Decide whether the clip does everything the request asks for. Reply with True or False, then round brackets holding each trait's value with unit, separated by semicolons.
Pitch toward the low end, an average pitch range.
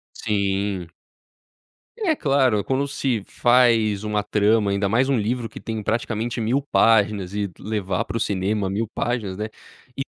True (110 Hz; 3.0 semitones)